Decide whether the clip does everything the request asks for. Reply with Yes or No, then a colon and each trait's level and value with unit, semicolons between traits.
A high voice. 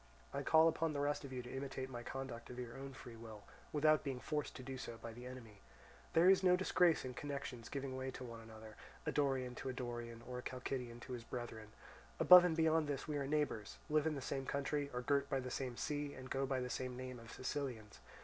No: low, 130 Hz